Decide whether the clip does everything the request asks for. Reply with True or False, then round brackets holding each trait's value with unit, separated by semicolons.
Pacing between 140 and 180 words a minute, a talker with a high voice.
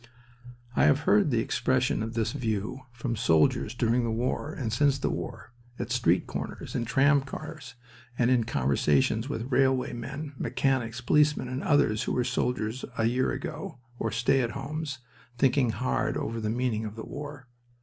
False (170 wpm; 125 Hz)